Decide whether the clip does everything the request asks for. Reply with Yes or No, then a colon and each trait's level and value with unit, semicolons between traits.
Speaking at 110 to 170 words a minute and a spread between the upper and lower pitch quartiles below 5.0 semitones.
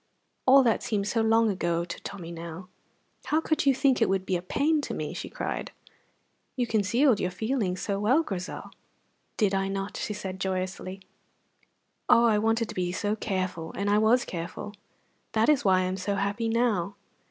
No: average, 185 wpm; average, 3.7 semitones